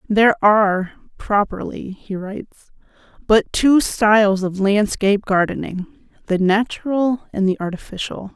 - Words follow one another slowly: Yes, slow, 115 wpm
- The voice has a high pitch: Yes, high, 205 Hz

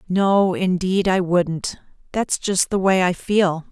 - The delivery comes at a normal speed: Yes, average, 160 wpm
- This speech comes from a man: No, female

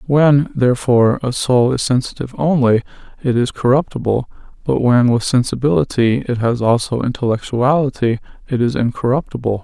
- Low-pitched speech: Yes, low, 125 Hz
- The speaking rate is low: Yes, slow, 130 wpm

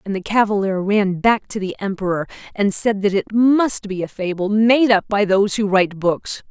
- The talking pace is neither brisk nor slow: No, fast, 210 wpm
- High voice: Yes, high, 205 Hz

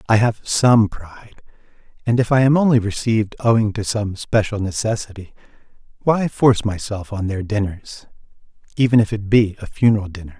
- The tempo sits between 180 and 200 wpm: No, average, 160 wpm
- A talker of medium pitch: No, low, 110 Hz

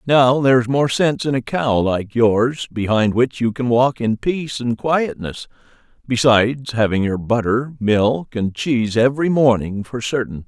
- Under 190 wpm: Yes, average, 165 wpm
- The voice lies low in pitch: Yes, low, 120 Hz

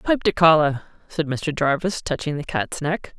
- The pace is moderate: Yes, average, 190 wpm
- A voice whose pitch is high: No, medium, 155 Hz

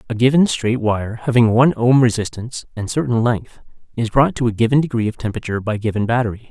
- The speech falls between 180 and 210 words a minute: Yes, fast, 205 wpm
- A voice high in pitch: No, low, 115 Hz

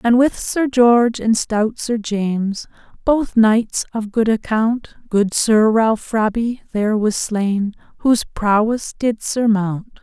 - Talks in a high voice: Yes, high, 220 Hz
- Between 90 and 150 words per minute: Yes, average, 145 wpm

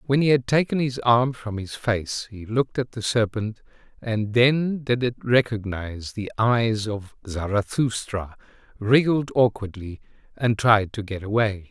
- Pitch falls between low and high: No, low, 115 Hz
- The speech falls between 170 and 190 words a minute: No, average, 155 wpm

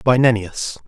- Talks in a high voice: No, low, 115 Hz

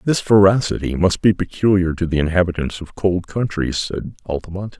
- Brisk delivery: No, average, 165 wpm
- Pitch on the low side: Yes, very low, 90 Hz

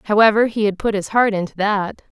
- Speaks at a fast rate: Yes, fast, 220 wpm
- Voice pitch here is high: Yes, high, 205 Hz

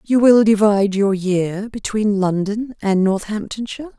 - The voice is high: Yes, high, 210 Hz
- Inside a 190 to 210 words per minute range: No, slow, 135 wpm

